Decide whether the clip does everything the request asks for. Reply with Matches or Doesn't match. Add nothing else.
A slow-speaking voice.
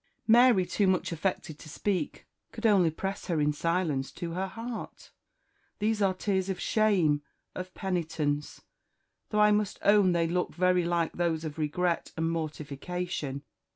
Doesn't match